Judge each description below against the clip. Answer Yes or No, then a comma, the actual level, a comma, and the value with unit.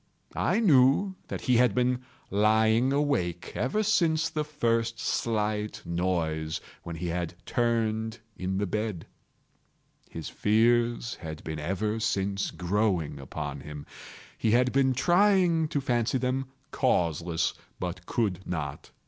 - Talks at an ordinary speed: No, slow, 130 wpm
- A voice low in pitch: Yes, low, 110 Hz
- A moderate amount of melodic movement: No, wide, 6.3 semitones